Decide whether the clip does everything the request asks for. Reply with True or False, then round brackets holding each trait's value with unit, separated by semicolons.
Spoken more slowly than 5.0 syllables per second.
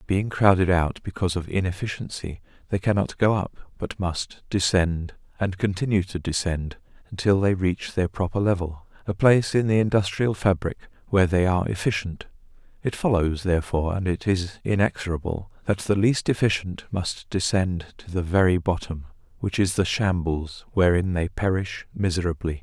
False (5.1 syllables/s)